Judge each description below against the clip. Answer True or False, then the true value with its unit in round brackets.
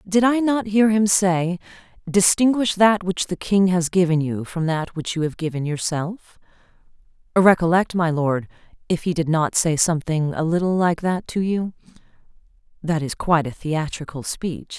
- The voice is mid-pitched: True (175 Hz)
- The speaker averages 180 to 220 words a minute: False (160 wpm)